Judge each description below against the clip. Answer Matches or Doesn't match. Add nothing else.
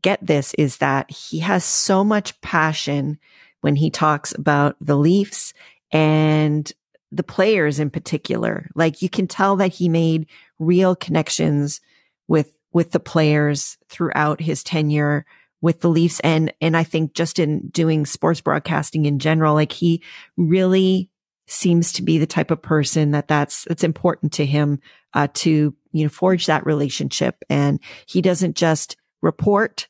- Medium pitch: Matches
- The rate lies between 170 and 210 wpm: Doesn't match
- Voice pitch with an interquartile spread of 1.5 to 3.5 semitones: Matches